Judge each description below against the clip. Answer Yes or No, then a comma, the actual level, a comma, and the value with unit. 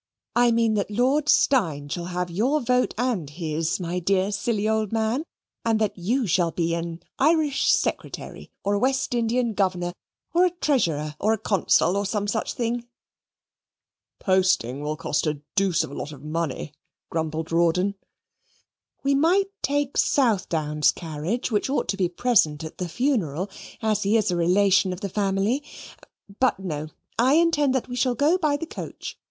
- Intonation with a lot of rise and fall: Yes, wide, 6.6 semitones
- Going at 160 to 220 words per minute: Yes, average, 170 wpm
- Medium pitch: No, high, 200 Hz